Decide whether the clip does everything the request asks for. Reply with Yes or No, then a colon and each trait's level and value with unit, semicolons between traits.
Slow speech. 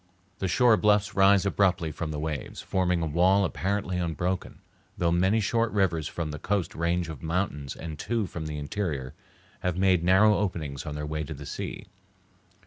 No: average, 180 wpm